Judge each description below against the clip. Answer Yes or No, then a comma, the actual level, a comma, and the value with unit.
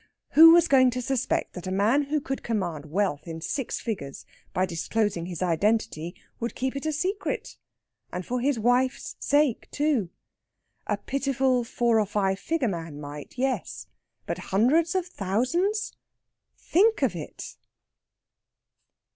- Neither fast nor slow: Yes, average, 145 wpm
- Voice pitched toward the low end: No, high, 235 Hz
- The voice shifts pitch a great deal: Yes, wide, 7.1 semitones